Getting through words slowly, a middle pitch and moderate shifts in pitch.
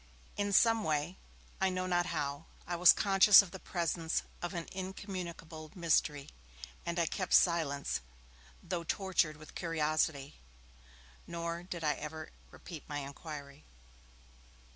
Yes: slow, 130 wpm; medium, 170 Hz; average, 3.0 semitones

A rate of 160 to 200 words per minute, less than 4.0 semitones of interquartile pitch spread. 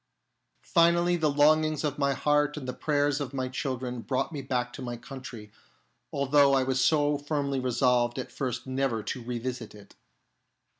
Yes: average, 165 wpm; average, 2.7 semitones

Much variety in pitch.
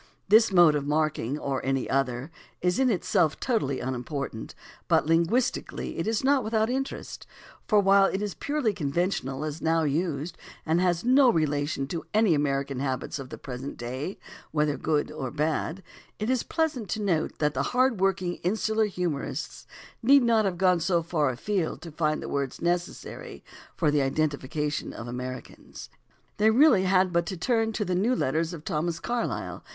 Yes: wide, 6.3 semitones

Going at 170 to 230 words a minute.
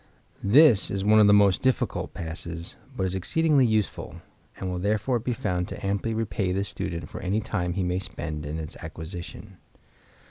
Yes: average, 180 wpm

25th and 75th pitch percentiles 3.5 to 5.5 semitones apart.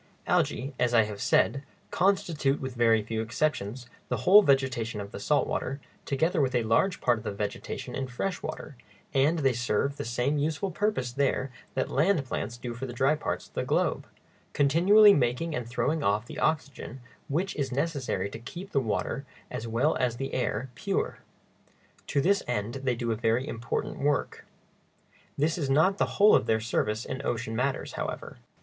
Yes: average, 4.4 semitones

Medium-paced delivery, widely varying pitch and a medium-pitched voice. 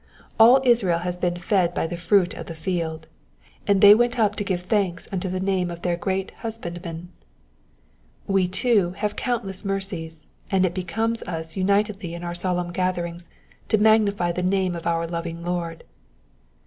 No: average, 170 wpm; average, 2.7 semitones; medium, 180 Hz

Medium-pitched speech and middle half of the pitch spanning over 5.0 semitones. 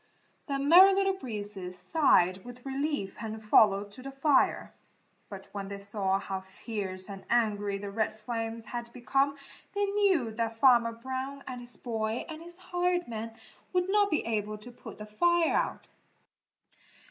No: high, 235 Hz; wide, 5.4 semitones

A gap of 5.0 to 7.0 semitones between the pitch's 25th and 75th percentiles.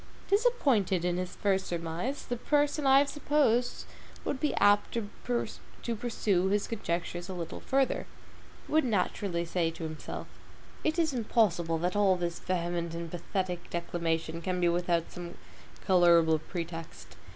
Yes: wide, 5.6 semitones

